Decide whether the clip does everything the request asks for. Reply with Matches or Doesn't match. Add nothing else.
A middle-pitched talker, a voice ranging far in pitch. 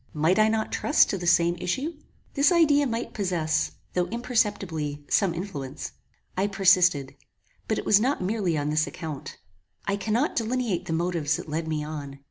Matches